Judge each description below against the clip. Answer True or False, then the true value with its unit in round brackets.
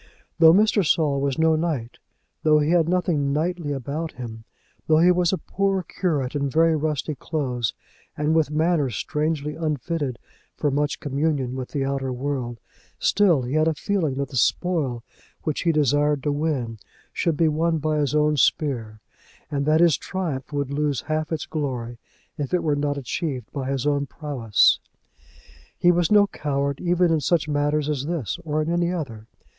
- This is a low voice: False (150 Hz)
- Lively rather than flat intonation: False (2.9 semitones)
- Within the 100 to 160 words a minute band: False (175 wpm)